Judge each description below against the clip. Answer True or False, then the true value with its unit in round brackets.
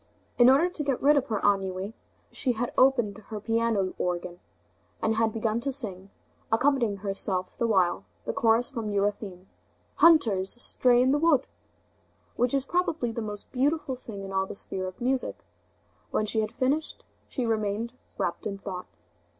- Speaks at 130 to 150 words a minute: False (165 wpm)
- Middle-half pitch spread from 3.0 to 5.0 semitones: True (4.5 semitones)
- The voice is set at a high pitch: True (225 Hz)